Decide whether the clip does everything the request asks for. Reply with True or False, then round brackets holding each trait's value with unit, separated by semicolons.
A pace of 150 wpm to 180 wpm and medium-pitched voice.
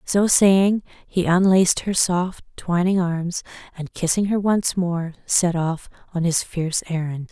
True (155 wpm; 180 Hz)